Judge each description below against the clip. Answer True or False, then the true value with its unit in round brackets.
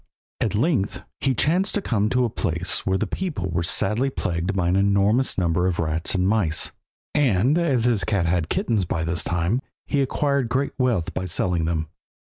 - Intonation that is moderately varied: False (6.6 semitones)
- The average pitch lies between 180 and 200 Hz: False (100 Hz)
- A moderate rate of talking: True (195 wpm)